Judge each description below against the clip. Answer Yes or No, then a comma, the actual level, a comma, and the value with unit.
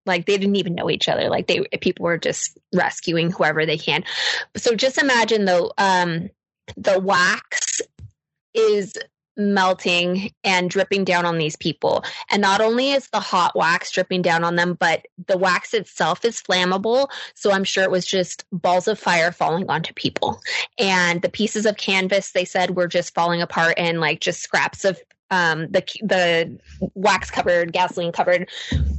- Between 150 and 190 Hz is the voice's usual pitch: Yes, medium, 185 Hz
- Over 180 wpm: No, average, 175 wpm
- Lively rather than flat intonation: No, average, 3.1 semitones